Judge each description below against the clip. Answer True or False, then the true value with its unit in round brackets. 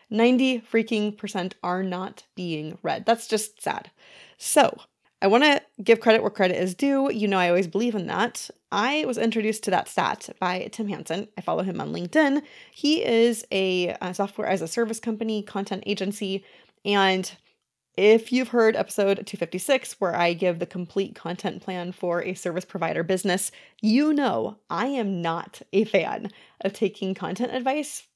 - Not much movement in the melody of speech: False (3.7 semitones)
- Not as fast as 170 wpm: False (175 wpm)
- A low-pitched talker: False (205 Hz)